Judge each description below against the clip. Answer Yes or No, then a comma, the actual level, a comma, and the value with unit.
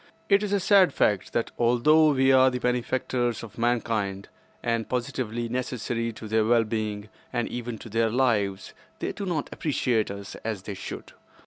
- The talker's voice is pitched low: Yes, low, 120 Hz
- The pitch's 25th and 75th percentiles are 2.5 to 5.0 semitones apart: Yes, average, 2.9 semitones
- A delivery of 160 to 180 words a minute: Yes, average, 175 wpm